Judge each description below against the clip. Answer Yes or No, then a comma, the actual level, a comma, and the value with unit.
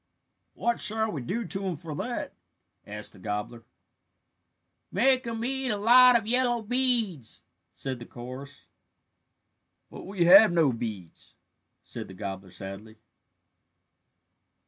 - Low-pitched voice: No, medium, 175 Hz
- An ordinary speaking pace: No, slow, 125 wpm